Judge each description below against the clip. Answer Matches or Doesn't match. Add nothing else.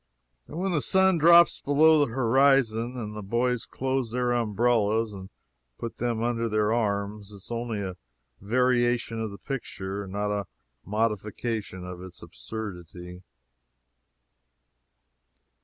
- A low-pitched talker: Matches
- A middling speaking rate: Doesn't match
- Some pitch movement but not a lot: Matches